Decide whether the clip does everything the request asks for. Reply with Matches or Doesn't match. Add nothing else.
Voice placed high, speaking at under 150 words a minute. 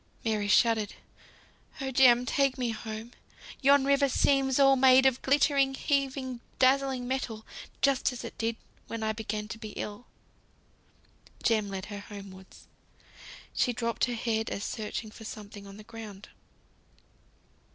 Matches